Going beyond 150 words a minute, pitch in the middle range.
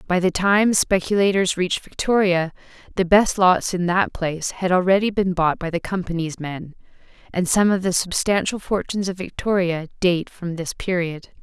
Yes: average, 170 wpm; medium, 180 Hz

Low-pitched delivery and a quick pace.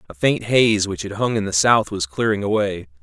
Yes: low, 100 Hz; fast, 240 wpm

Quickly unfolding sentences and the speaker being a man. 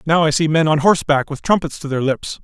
Yes: fast, 270 wpm; male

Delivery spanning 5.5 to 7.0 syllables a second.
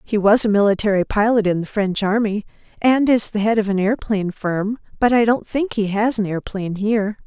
Yes: 5.8 syllables/s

